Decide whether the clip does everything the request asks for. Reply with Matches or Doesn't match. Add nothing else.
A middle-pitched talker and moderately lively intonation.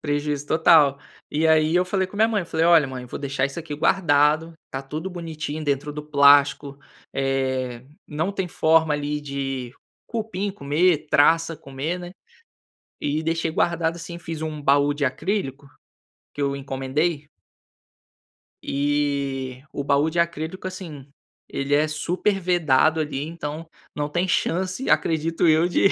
Matches